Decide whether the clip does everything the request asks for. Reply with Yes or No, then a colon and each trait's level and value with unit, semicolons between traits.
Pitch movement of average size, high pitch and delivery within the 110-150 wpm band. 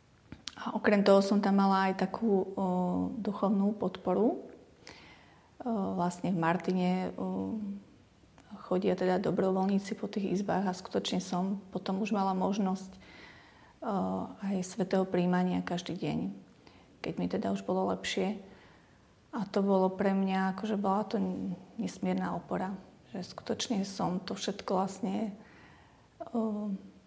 No: narrow, 2.0 semitones; high, 195 Hz; average, 130 wpm